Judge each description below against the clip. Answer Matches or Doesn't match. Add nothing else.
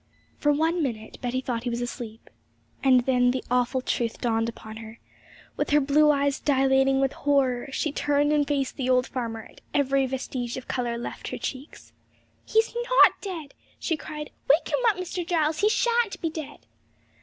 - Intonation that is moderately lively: Matches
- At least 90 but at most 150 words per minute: Doesn't match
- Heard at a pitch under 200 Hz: Doesn't match